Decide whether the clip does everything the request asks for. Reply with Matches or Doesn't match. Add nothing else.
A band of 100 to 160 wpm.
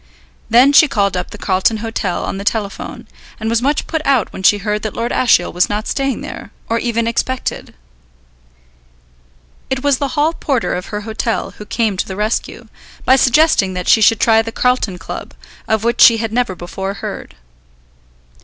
Doesn't match